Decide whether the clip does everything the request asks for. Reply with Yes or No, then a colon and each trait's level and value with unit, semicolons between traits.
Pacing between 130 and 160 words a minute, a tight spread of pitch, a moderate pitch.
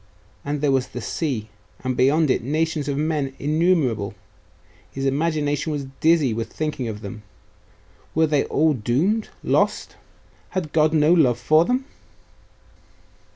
No: average, 140 wpm; average, 3.7 semitones; medium, 145 Hz